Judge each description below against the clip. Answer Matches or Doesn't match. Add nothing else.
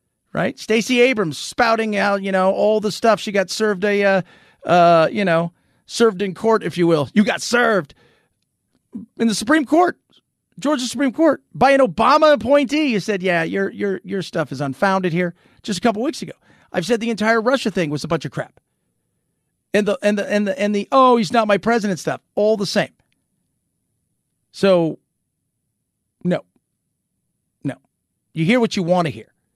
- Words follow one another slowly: Doesn't match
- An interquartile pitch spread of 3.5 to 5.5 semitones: Matches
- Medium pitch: Doesn't match